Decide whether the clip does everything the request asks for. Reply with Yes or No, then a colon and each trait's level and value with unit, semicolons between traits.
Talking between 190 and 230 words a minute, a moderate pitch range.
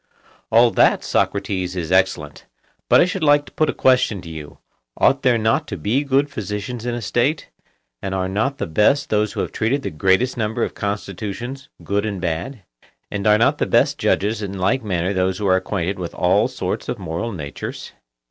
Yes: average, 200 wpm; average, 4.8 semitones